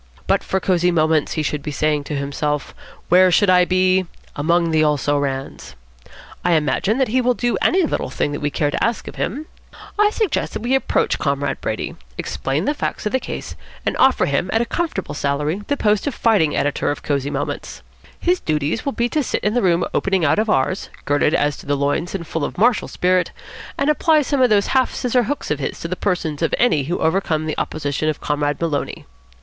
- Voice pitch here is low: No, medium, 175 Hz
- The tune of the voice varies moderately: No, wide, 7.6 semitones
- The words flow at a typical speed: No, fast, 215 wpm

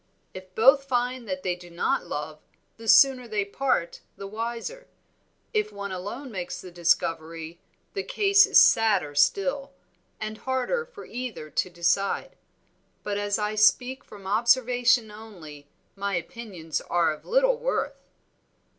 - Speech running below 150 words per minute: Yes, average, 140 wpm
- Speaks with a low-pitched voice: No, high, 210 Hz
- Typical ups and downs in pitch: No, wide, 6.2 semitones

